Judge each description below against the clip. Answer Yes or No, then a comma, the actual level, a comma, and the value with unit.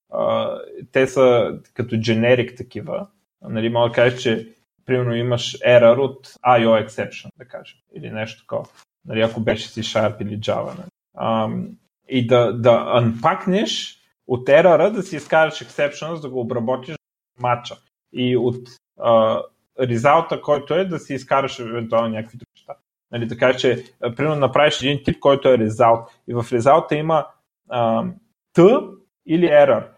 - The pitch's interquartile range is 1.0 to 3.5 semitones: No, average, 4.7 semitones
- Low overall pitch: Yes, low, 125 Hz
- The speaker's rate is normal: Yes, average, 155 wpm